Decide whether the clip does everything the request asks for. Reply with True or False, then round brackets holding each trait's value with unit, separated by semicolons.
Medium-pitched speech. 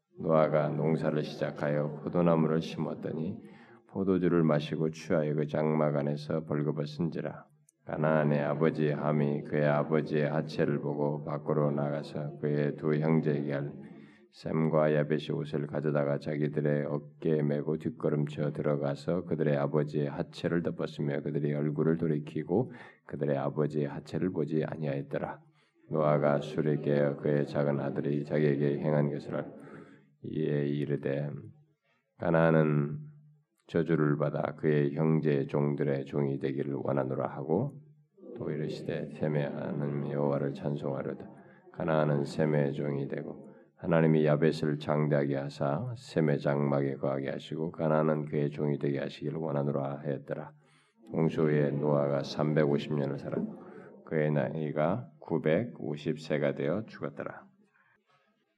False (75 Hz)